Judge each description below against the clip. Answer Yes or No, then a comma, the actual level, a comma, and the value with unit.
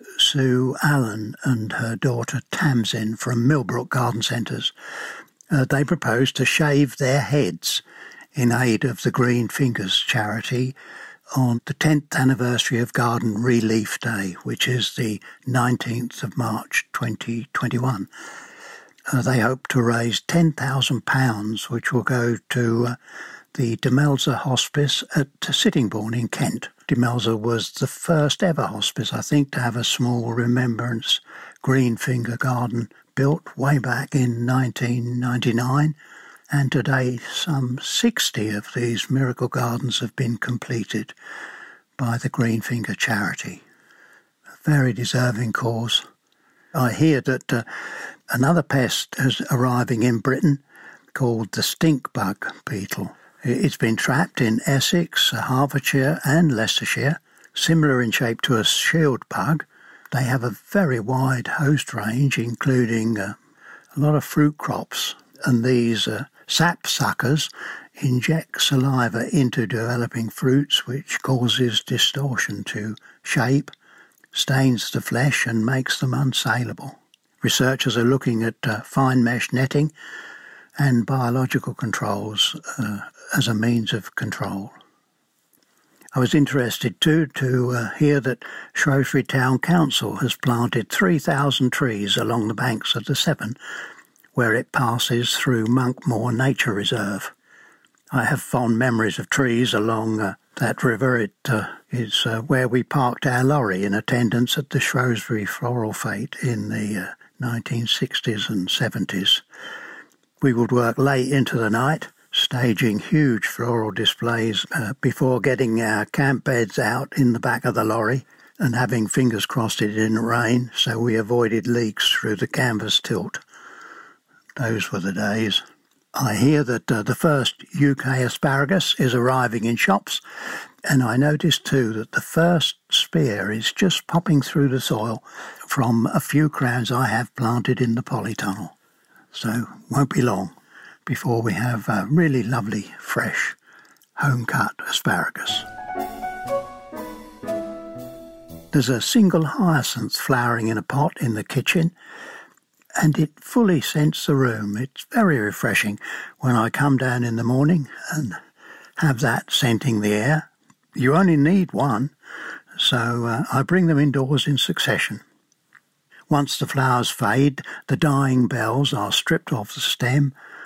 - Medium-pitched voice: No, low, 125 Hz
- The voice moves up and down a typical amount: Yes, average, 3.2 semitones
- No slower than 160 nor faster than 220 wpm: No, slow, 135 wpm